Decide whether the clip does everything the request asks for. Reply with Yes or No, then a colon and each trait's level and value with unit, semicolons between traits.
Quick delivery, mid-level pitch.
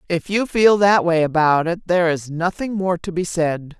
Yes: fast, 220 wpm; medium, 175 Hz